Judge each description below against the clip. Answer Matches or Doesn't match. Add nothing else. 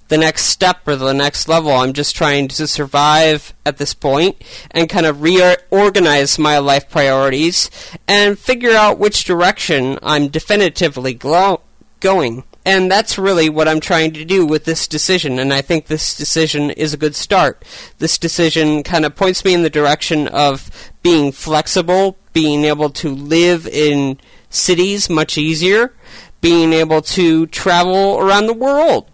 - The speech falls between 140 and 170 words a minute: Matches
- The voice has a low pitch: Doesn't match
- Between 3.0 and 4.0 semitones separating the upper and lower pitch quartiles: Matches